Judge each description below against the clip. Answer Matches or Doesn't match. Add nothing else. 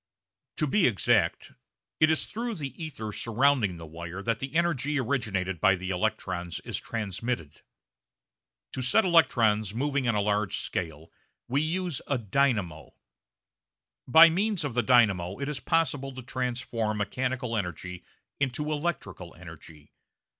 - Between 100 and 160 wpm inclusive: Matches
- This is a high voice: Doesn't match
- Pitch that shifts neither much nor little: Doesn't match